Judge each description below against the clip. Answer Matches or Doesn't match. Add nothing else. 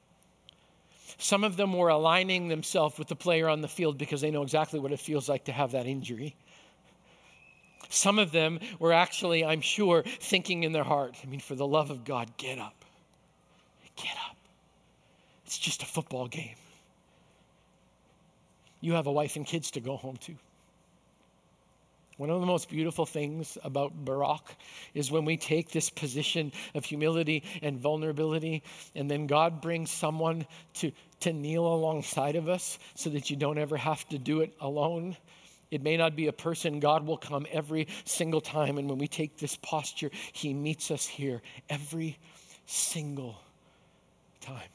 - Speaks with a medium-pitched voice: Matches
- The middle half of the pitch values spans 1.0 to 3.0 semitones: Matches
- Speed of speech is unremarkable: Matches